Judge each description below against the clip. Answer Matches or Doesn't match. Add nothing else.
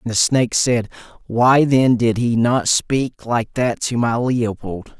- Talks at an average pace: Matches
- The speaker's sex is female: Doesn't match